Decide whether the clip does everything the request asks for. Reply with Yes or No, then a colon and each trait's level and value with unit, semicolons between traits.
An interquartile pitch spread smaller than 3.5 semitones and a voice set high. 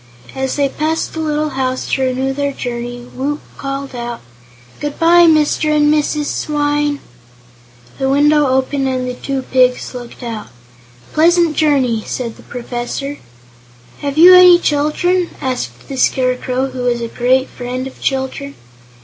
Yes: average, 2.9 semitones; very high, 270 Hz